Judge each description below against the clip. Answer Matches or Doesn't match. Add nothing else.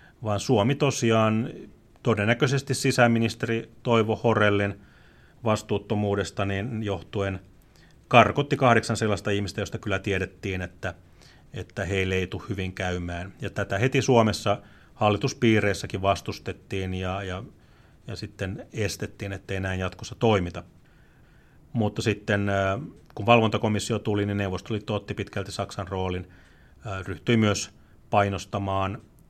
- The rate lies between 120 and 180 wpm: Doesn't match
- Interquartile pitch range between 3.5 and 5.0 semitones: Doesn't match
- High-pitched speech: Doesn't match